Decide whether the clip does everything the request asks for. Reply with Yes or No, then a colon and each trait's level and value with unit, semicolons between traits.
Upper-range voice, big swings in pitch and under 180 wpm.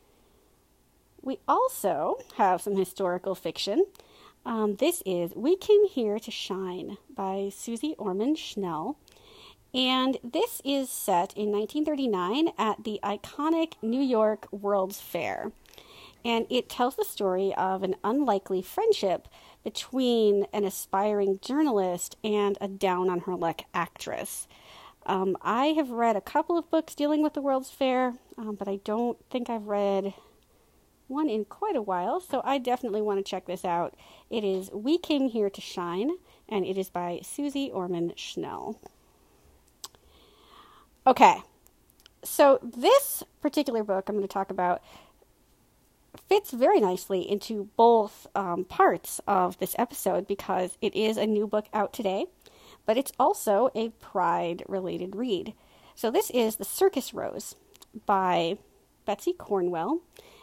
Yes: high, 215 Hz; wide, 6.4 semitones; average, 140 wpm